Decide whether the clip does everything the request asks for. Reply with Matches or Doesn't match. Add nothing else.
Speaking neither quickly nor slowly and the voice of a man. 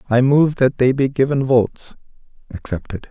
Matches